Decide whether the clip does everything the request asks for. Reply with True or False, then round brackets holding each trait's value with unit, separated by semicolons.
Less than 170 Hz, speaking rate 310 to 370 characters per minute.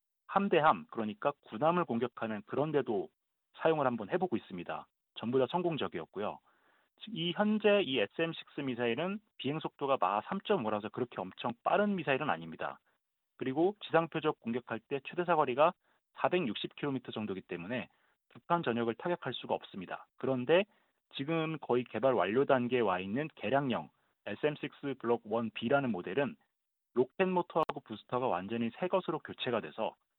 True (135 Hz; 330 characters per minute)